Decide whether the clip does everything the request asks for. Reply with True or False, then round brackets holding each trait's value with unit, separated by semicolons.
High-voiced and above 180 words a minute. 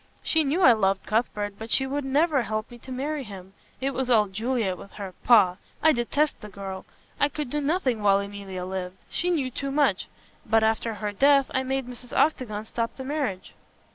True (240 Hz; 200 wpm)